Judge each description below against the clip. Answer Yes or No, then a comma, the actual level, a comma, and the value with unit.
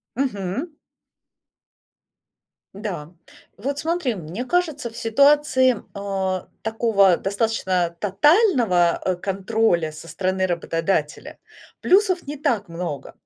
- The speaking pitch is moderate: No, high, 210 Hz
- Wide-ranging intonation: Yes, wide, 7.1 semitones